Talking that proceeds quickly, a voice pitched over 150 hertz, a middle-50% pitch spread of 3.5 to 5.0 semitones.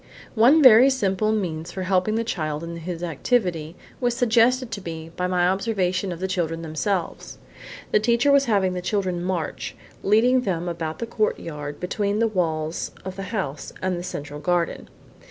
No: average, 170 wpm; medium, 185 Hz; average, 4.6 semitones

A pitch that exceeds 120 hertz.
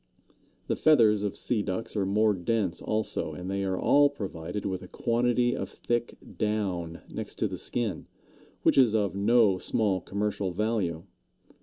No: low, 105 Hz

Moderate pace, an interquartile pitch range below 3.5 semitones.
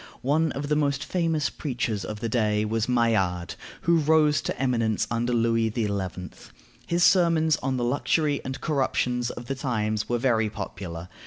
No: average, 165 wpm; average, 5.2 semitones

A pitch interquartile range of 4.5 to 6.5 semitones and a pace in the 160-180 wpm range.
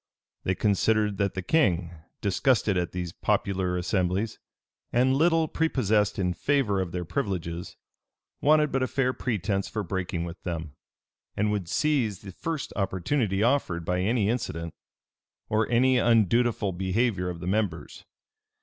No: average, 5.0 semitones; average, 140 wpm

